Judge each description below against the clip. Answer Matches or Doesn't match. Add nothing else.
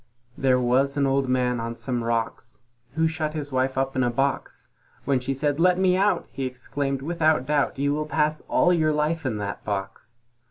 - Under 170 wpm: Doesn't match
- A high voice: Doesn't match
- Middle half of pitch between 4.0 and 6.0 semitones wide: Doesn't match